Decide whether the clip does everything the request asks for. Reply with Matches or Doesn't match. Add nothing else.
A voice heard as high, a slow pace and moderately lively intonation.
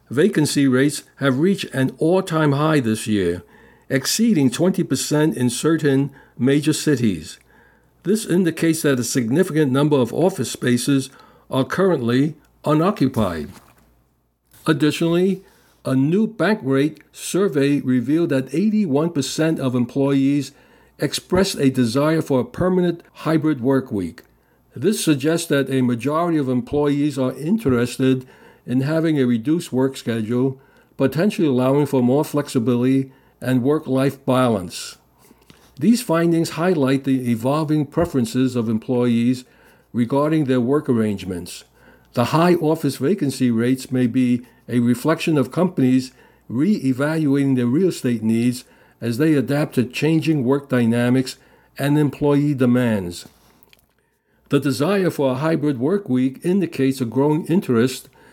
Doesn't match